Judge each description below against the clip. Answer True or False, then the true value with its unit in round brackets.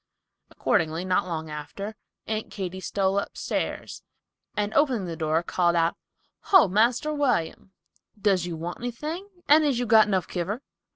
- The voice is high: True (195 Hz)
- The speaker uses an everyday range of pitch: False (5.7 semitones)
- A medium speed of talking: True (150 wpm)